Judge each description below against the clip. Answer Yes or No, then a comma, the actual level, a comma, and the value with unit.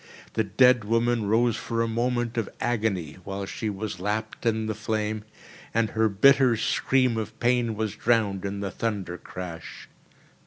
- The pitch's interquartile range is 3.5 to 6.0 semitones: No, narrow, 2.6 semitones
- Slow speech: No, average, 155 wpm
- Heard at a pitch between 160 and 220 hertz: No, low, 110 Hz